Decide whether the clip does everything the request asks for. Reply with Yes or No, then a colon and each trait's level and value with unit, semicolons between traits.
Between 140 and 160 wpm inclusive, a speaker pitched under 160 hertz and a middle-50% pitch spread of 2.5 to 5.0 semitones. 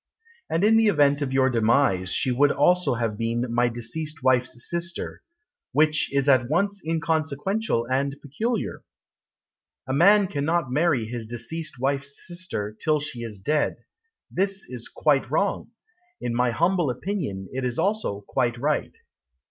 No: average, 150 wpm; medium, 140 Hz; wide, 5.6 semitones